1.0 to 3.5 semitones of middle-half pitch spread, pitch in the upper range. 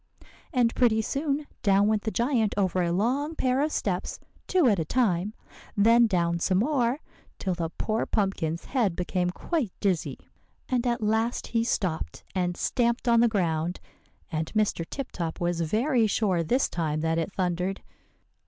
No: average, 5.2 semitones; high, 210 Hz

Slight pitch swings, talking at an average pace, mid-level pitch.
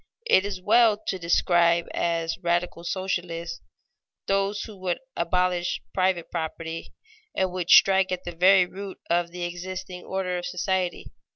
Yes: narrow, 1.7 semitones; average, 145 wpm; medium, 180 Hz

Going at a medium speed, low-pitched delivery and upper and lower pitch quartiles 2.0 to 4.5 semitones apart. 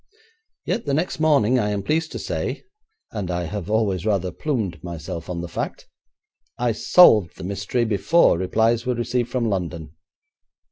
No: average, 160 wpm; low, 105 Hz; average, 5.3 semitones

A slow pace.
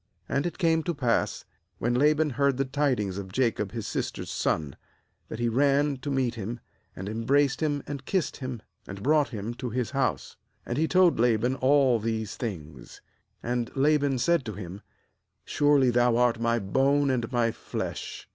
No: average, 180 wpm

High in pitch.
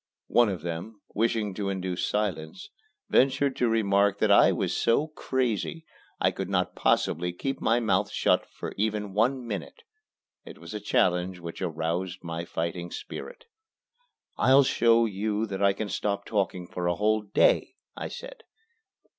No: low, 100 Hz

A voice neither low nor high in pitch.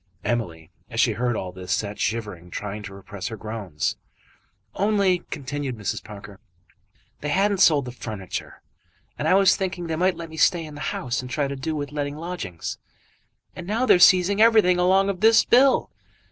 Yes: medium, 145 Hz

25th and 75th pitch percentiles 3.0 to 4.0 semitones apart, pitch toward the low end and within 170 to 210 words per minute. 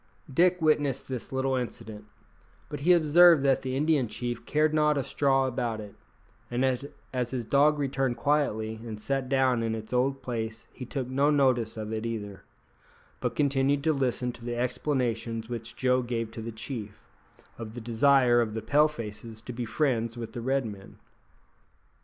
Yes: average, 3.3 semitones; low, 125 Hz; average, 175 wpm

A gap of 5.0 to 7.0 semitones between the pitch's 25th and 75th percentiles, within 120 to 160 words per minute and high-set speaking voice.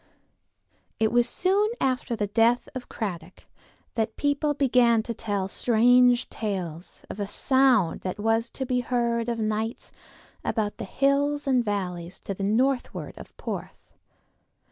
No: average, 3.5 semitones; average, 145 wpm; high, 235 Hz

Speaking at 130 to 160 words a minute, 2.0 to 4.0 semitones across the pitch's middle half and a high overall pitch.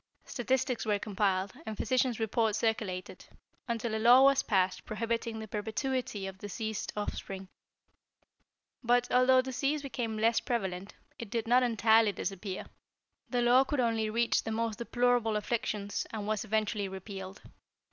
Yes: average, 140 wpm; average, 2.9 semitones; high, 220 Hz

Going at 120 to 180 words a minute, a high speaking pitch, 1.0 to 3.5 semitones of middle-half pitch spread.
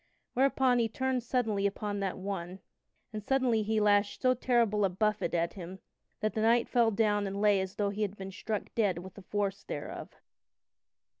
No: average, 190 wpm; high, 210 Hz; narrow, 2.5 semitones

